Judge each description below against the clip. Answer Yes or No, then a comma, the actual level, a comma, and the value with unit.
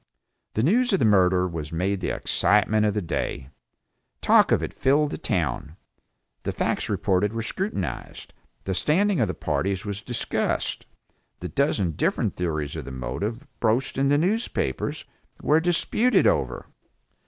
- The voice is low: Yes, low, 105 Hz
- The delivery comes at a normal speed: Yes, average, 155 wpm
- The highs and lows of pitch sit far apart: Yes, wide, 8.6 semitones